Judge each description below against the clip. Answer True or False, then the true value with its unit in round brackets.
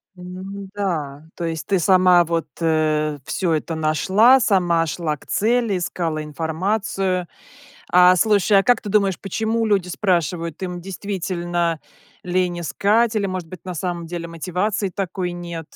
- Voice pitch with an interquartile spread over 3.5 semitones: False (2.8 semitones)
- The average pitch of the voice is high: False (180 Hz)